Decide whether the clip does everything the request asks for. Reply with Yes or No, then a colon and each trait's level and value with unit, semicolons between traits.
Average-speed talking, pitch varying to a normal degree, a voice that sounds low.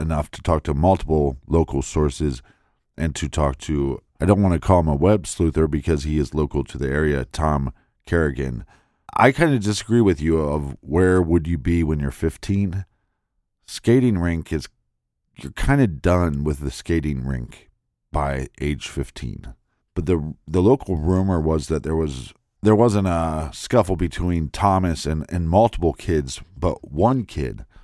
Yes: average, 170 wpm; average, 4.0 semitones; very low, 80 Hz